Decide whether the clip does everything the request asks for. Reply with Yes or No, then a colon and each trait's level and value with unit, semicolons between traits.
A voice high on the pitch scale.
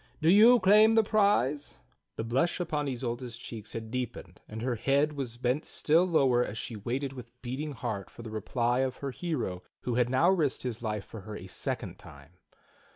No: low, 125 Hz